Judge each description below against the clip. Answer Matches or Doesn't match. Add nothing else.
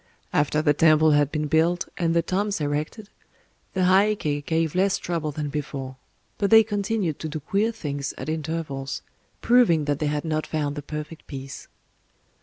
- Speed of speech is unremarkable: Matches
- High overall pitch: Doesn't match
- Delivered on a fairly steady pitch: Doesn't match